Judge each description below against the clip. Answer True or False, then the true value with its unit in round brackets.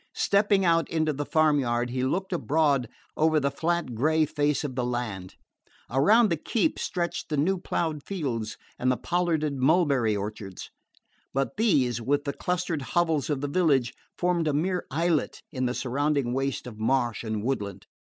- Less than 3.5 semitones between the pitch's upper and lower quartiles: False (4.9 semitones)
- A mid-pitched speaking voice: True (145 Hz)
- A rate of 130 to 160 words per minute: False (170 wpm)